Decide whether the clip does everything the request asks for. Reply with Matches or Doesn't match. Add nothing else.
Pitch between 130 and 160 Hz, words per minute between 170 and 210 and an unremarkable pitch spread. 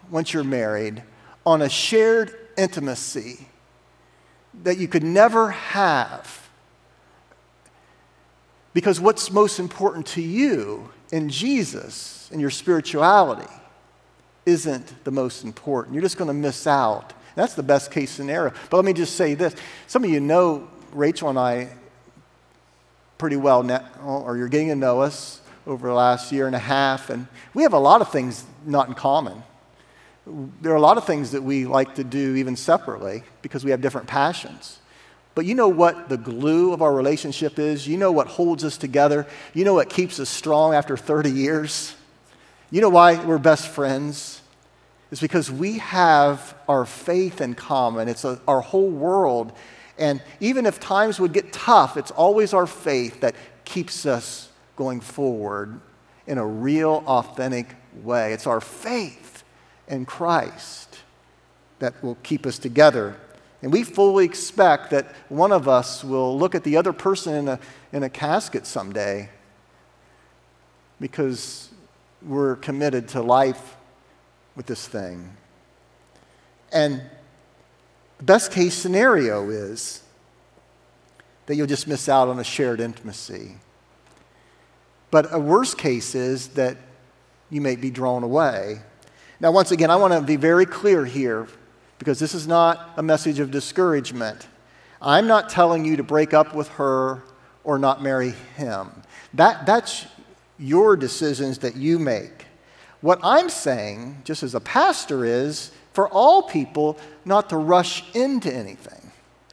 Doesn't match